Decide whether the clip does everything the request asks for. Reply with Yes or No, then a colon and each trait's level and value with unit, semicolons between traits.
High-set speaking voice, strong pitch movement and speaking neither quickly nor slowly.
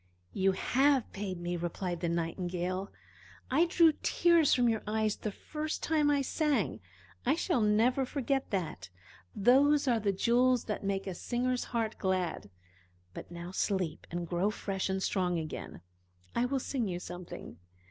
Yes: high, 210 Hz; wide, 6.1 semitones; average, 160 wpm